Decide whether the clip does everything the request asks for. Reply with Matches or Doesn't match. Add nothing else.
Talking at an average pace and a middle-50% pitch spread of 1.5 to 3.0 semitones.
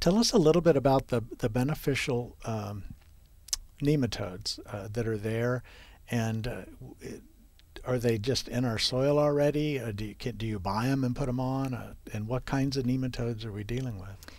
Doesn't match